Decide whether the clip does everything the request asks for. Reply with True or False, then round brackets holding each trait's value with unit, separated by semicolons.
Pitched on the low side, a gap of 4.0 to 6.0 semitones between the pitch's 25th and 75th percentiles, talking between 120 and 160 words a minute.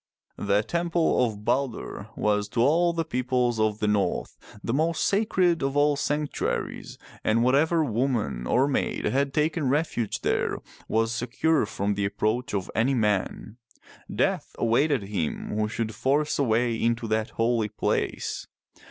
True (120 Hz; 5.1 semitones; 150 wpm)